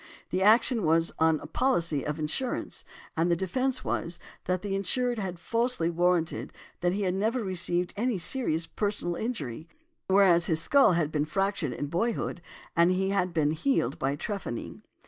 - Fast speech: No, average, 165 wpm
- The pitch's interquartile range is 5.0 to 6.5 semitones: No, average, 4.4 semitones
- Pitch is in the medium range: Yes, medium, 180 Hz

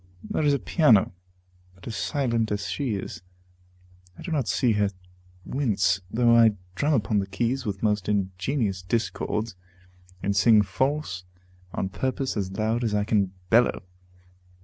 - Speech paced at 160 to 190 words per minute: No, average, 150 wpm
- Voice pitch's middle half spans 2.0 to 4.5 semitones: Yes, average, 4.0 semitones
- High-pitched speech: No, low, 110 Hz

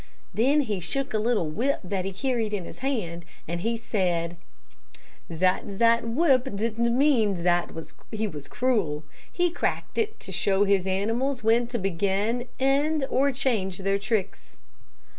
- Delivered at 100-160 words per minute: Yes, average, 155 wpm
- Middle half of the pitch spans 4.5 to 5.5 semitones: Yes, average, 5.1 semitones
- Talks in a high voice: Yes, high, 220 Hz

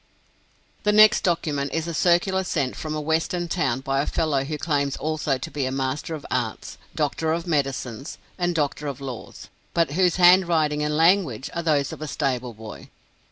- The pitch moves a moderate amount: Yes, average, 3.7 semitones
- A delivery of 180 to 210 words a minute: Yes, average, 185 wpm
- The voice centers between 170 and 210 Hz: No, medium, 150 Hz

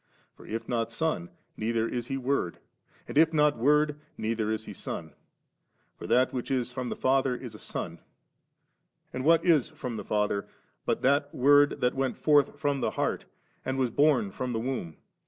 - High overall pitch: No, low, 130 Hz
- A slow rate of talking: No, average, 185 wpm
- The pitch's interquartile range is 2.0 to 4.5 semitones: Yes, average, 4.0 semitones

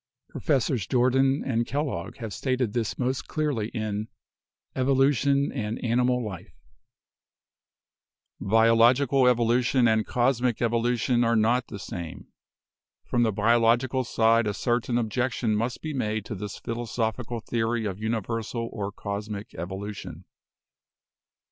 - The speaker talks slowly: Yes, slow, 115 wpm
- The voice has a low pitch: Yes, low, 115 Hz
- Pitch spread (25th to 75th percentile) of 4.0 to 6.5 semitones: No, narrow, 2.5 semitones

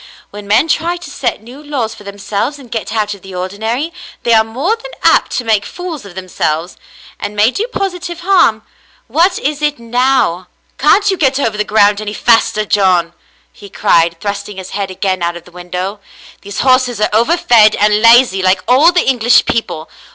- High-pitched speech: Yes, high, 220 Hz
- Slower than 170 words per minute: No, average, 195 wpm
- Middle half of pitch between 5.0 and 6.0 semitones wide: Yes, average, 5.3 semitones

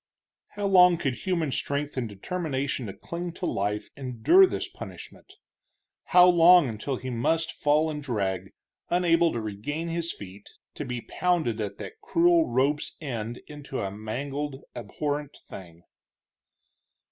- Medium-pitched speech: Yes, medium, 145 Hz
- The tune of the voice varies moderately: No, wide, 6.7 semitones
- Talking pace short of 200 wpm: Yes, average, 140 wpm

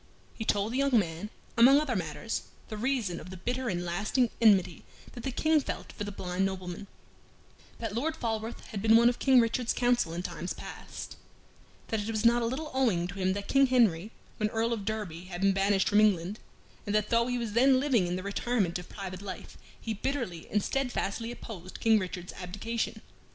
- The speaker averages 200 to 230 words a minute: Yes, fast, 205 wpm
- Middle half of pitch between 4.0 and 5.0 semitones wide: Yes, average, 4.3 semitones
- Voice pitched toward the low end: No, high, 215 Hz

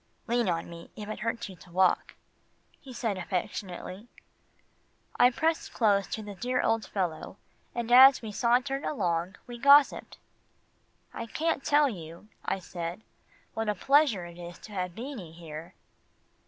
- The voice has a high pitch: Yes, high, 215 Hz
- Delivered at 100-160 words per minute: Yes, average, 155 wpm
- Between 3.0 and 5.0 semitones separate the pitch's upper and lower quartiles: No, wide, 5.6 semitones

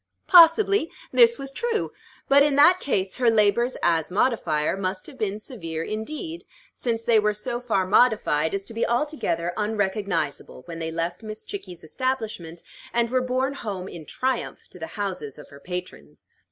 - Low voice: No, high, 215 Hz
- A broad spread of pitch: Yes, wide, 6.4 semitones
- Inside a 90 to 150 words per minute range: No, average, 165 wpm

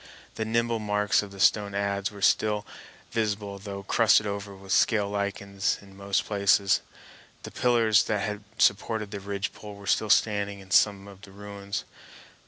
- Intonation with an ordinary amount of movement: No, narrow, 1.1 semitones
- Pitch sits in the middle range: No, low, 100 Hz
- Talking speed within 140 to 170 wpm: Yes, average, 165 wpm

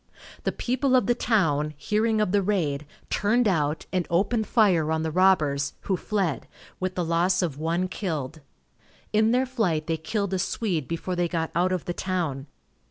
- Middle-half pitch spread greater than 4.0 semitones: Yes, average, 4.7 semitones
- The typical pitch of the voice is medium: Yes, medium, 180 Hz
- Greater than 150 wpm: Yes, average, 180 wpm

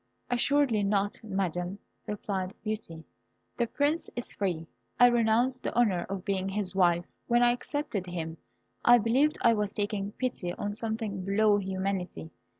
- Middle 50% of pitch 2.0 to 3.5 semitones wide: No, average, 3.9 semitones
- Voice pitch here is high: Yes, high, 205 Hz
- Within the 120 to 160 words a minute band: Yes, average, 150 wpm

